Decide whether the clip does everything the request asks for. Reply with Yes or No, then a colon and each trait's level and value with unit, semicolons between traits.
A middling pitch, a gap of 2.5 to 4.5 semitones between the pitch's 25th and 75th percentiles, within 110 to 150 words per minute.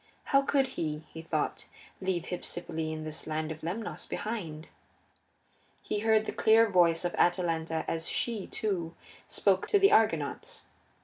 No: medium, 175 Hz; average, 5.2 semitones; average, 145 wpm